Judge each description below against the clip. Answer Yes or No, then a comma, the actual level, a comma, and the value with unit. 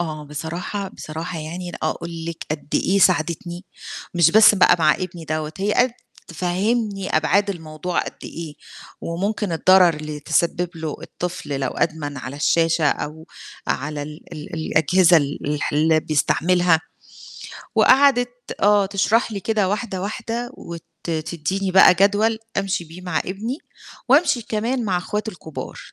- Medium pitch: Yes, medium, 175 Hz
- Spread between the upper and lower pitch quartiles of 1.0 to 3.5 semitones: No, average, 4.1 semitones